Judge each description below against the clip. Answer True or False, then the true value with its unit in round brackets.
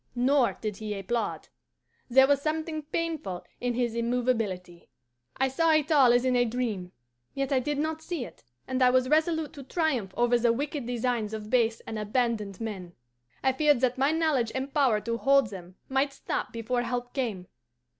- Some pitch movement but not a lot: True (3.6 semitones)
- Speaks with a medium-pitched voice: False (250 Hz)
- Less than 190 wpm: True (180 wpm)